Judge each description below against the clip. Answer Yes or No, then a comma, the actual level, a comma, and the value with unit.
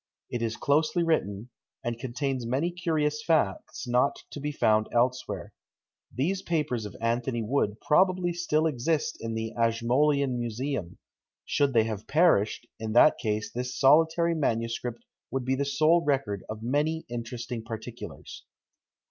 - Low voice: Yes, low, 125 Hz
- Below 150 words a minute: Yes, average, 140 wpm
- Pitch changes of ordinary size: Yes, average, 4.7 semitones